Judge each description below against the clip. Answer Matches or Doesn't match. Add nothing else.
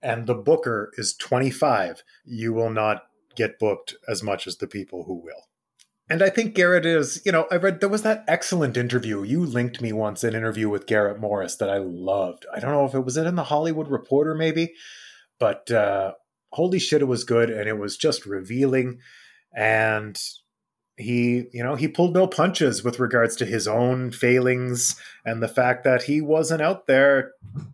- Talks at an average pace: Matches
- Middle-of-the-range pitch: Doesn't match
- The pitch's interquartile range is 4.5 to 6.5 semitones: Matches